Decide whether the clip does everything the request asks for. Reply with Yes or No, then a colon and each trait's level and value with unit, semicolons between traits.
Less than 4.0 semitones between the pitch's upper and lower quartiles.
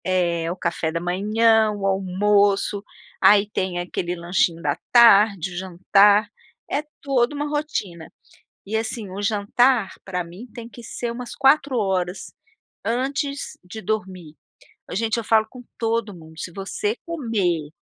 No: average, 4.3 semitones